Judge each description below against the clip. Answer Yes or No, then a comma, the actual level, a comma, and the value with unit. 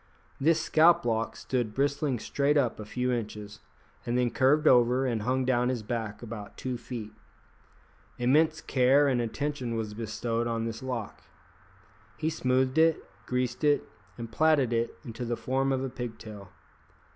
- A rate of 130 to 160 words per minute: Yes, average, 155 wpm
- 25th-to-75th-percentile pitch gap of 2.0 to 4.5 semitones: Yes, average, 2.9 semitones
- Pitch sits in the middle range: No, low, 125 Hz